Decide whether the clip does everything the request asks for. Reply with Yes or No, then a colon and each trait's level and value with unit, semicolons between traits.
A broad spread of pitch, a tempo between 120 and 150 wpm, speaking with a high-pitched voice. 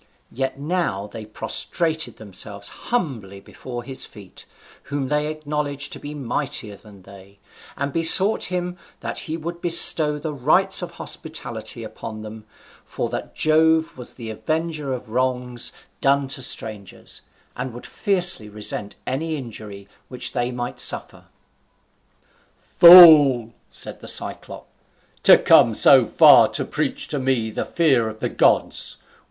No: wide, 6.0 semitones; average, 140 wpm; low, 135 Hz